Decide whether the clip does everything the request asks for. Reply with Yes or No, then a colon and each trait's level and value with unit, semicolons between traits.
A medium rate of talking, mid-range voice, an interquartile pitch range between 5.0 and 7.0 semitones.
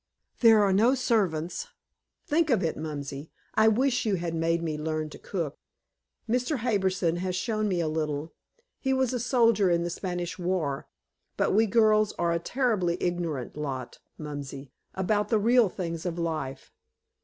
Yes: average, 165 wpm; medium, 180 Hz; wide, 5.6 semitones